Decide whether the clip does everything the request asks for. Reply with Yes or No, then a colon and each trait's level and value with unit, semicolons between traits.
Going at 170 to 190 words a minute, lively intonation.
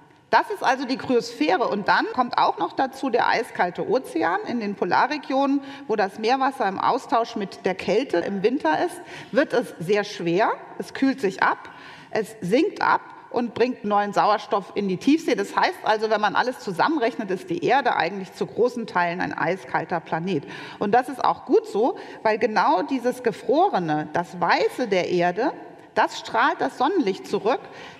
Yes: average, 175 wpm; wide, 6.0 semitones